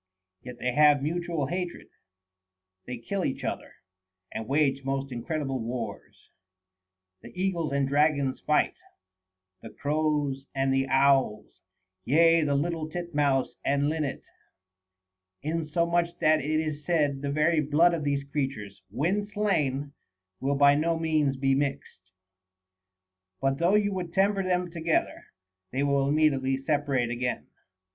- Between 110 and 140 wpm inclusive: Yes, slow, 135 wpm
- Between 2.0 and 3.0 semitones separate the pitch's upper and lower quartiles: No, average, 3.4 semitones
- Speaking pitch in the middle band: Yes, medium, 145 Hz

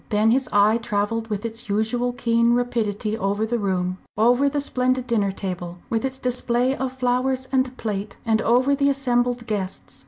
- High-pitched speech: Yes, high, 235 Hz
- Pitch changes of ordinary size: Yes, average, 3.2 semitones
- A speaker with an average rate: Yes, average, 175 wpm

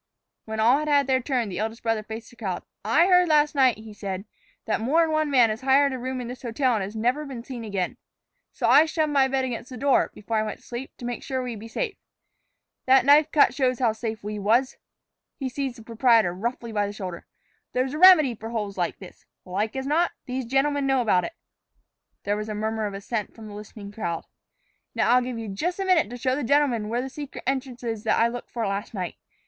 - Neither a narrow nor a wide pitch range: Yes, average, 3.8 semitones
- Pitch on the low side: No, high, 240 Hz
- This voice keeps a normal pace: No, fast, 240 wpm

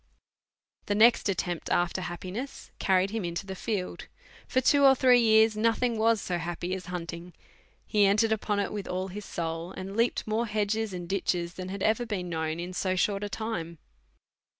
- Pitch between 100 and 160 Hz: No, high, 195 Hz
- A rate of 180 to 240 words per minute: Yes, average, 185 wpm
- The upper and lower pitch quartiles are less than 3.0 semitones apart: No, average, 3.7 semitones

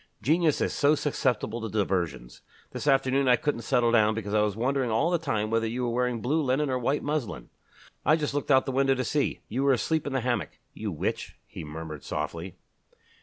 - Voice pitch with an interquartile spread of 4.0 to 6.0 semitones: Yes, average, 4.5 semitones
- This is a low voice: Yes, low, 125 Hz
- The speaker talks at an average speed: No, fast, 220 wpm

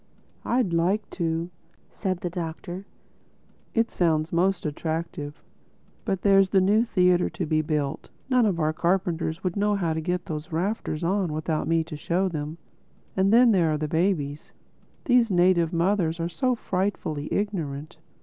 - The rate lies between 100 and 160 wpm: Yes, average, 155 wpm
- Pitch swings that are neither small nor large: Yes, average, 3.5 semitones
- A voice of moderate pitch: Yes, medium, 175 Hz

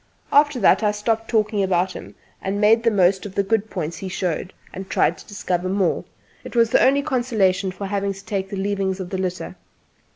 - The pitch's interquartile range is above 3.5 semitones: No, narrow, 2.6 semitones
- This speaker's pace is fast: Yes, fast, 215 wpm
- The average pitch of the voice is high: Yes, high, 200 Hz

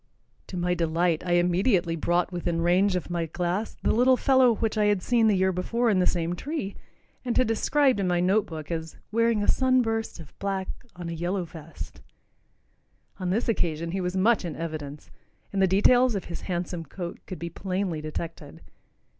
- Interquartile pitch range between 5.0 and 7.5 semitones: No, average, 4.0 semitones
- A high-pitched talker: No, medium, 180 Hz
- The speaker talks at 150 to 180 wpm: No, average, 195 wpm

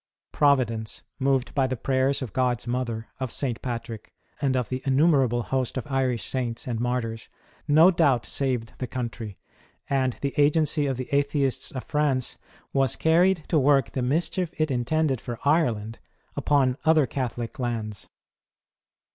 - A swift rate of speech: No, average, 155 wpm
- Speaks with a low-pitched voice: Yes, low, 130 Hz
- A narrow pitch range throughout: No, average, 3.0 semitones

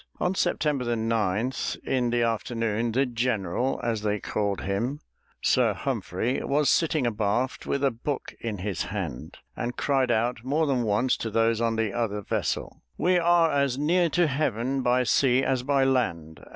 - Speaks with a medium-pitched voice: No, low, 120 Hz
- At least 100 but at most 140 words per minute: No, average, 165 wpm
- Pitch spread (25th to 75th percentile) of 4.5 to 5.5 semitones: No, average, 3.6 semitones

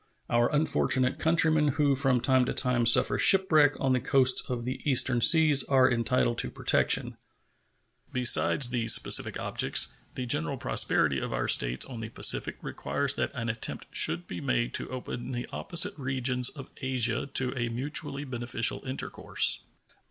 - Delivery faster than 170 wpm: No, average, 160 wpm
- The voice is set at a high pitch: No, low, 130 Hz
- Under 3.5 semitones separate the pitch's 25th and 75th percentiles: Yes, average, 2.7 semitones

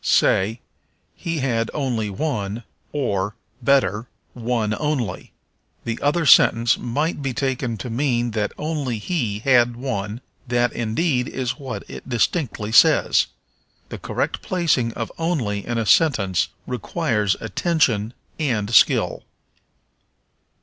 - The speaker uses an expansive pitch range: No, average, 4.2 semitones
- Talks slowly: Yes, slow, 120 wpm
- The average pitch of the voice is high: No, low, 120 Hz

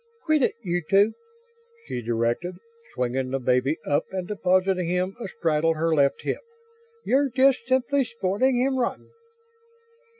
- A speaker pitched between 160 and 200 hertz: Yes, medium, 185 Hz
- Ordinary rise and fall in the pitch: No, wide, 8.5 semitones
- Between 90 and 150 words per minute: Yes, average, 140 wpm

